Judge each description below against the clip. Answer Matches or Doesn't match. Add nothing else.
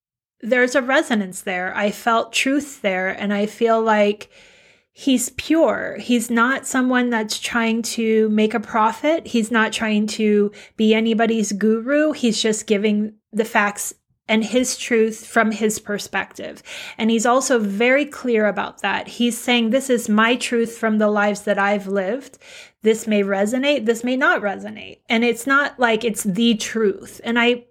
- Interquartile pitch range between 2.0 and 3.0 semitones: Matches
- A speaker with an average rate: Matches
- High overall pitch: Matches